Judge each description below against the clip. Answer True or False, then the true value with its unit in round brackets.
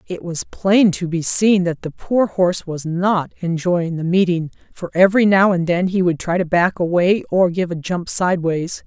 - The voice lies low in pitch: False (180 Hz)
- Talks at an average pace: False (210 wpm)